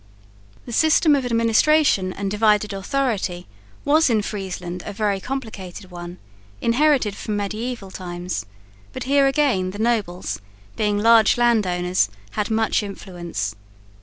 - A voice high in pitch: Yes, high, 210 Hz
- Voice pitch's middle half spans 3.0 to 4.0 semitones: No, average, 4.4 semitones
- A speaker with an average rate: No, slow, 130 wpm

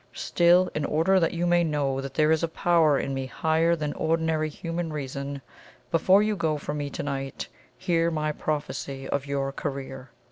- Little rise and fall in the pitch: No, average, 3.2 semitones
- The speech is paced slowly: No, average, 185 wpm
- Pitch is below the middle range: No, medium, 155 Hz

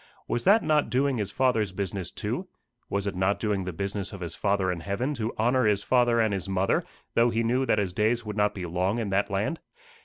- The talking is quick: Yes, fast, 235 wpm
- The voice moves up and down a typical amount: Yes, average, 3.4 semitones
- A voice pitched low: Yes, low, 105 Hz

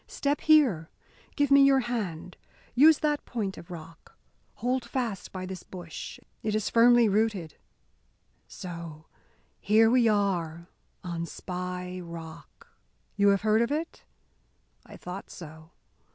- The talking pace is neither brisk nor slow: No, slow, 130 wpm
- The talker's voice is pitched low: No, high, 200 Hz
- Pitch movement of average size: No, wide, 5.9 semitones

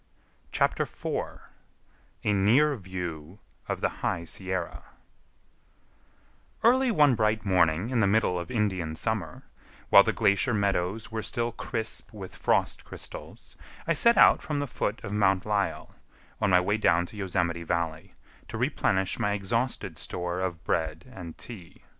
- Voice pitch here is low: Yes, low, 100 Hz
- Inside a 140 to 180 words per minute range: Yes, average, 145 wpm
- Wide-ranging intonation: No, average, 4.0 semitones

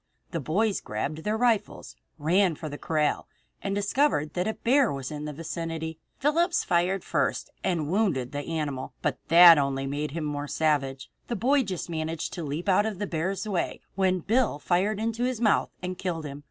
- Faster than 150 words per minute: Yes, average, 195 wpm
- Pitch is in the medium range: Yes, medium, 170 Hz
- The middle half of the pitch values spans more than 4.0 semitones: Yes, wide, 5.4 semitones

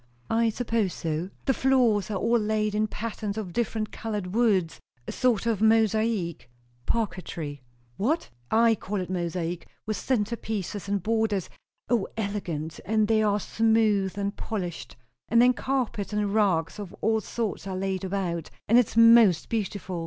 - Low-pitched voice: No, high, 210 Hz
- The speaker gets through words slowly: No, average, 160 wpm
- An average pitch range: Yes, average, 3.2 semitones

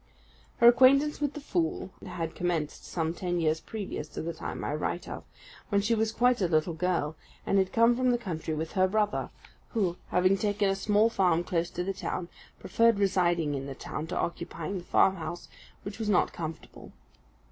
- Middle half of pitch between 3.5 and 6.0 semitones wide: Yes, average, 4.2 semitones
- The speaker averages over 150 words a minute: Yes, average, 190 wpm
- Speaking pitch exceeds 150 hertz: Yes, medium, 185 Hz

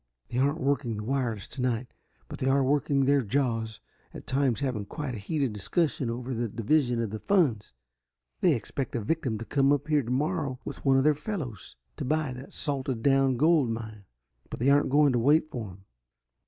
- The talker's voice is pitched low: Yes, low, 130 Hz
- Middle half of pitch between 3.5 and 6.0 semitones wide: Yes, average, 3.8 semitones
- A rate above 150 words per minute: Yes, average, 195 wpm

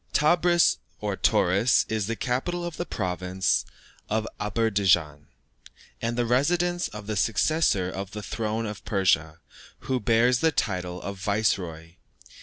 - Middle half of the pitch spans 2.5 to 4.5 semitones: No, average, 4.9 semitones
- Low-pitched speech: Yes, low, 105 Hz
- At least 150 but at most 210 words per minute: No, slow, 135 wpm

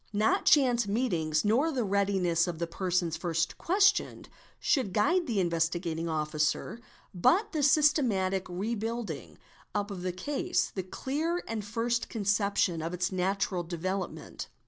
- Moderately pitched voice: No, high, 195 Hz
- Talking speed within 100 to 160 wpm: Yes, average, 140 wpm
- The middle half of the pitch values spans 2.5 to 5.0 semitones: No, wide, 5.5 semitones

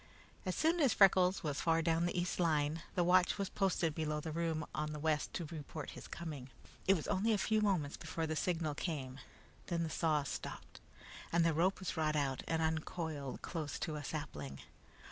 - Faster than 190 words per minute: Yes, average, 200 wpm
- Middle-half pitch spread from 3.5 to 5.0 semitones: No, average, 2.8 semitones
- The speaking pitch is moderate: Yes, medium, 160 Hz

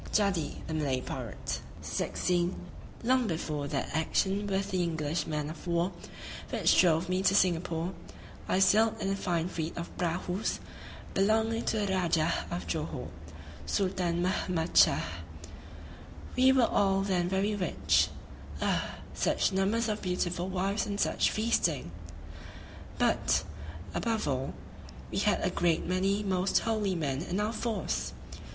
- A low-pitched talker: No, medium, 185 Hz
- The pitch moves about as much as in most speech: Yes, average, 3.5 semitones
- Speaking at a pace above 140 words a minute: No, slow, 135 wpm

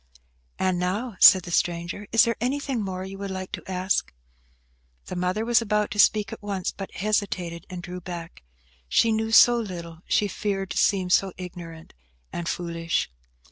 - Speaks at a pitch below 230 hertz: Yes, high, 190 Hz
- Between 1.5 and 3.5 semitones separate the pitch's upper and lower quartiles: Yes, average, 3.1 semitones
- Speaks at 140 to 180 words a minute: Yes, average, 175 wpm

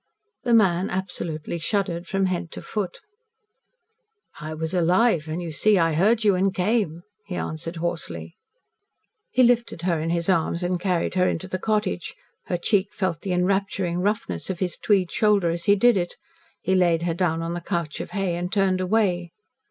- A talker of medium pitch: Yes, medium, 180 Hz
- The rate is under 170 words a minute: No, average, 185 wpm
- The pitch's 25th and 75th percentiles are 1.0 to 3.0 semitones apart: Yes, average, 2.7 semitones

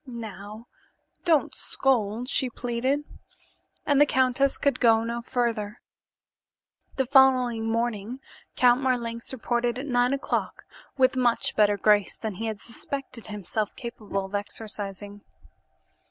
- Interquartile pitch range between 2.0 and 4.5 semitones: Yes, average, 3.1 semitones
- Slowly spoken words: Yes, slow, 125 wpm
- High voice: Yes, high, 235 Hz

